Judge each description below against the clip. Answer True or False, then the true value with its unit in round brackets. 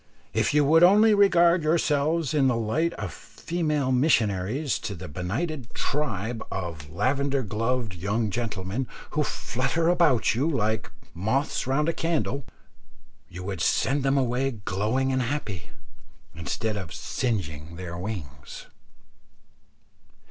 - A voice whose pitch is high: False (125 Hz)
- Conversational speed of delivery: False (125 wpm)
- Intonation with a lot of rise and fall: True (6.8 semitones)